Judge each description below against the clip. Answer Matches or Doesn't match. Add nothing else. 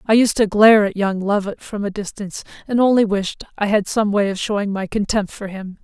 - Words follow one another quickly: Matches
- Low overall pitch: Doesn't match